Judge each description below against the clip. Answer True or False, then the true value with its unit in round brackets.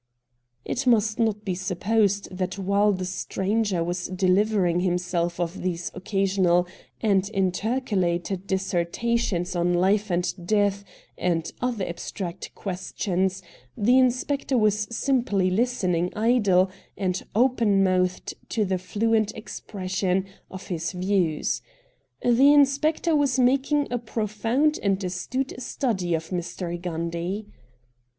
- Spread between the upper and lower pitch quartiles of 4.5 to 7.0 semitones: False (3.8 semitones)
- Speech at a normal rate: False (120 wpm)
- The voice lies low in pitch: False (195 Hz)